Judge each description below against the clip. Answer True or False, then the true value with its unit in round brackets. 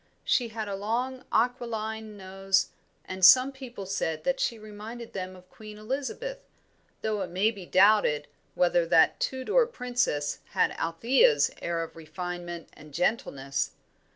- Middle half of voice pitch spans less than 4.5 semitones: False (5.2 semitones)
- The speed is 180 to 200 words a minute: False (140 wpm)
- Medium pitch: False (205 Hz)